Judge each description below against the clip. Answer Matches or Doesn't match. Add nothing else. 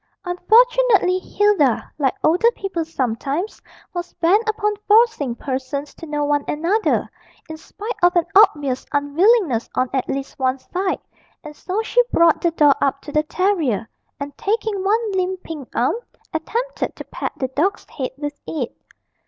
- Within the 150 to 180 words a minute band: Matches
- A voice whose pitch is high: Matches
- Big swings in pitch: Matches